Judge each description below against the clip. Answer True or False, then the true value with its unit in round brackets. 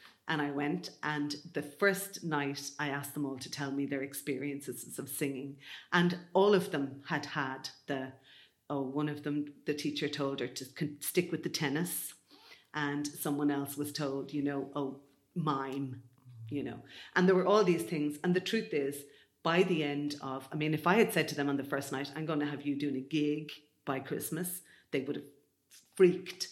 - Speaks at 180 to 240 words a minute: True (200 wpm)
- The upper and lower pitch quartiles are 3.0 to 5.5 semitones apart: False (2.4 semitones)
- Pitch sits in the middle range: True (145 Hz)